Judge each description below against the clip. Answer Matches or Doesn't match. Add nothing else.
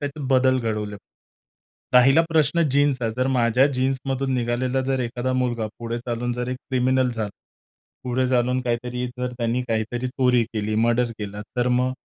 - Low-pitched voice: Matches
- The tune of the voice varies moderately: Doesn't match